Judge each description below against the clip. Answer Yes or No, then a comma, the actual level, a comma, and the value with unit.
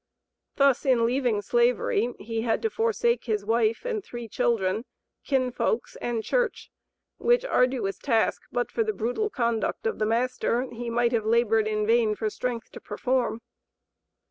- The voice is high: Yes, high, 240 Hz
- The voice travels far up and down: No, average, 3.7 semitones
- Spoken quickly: No, average, 155 wpm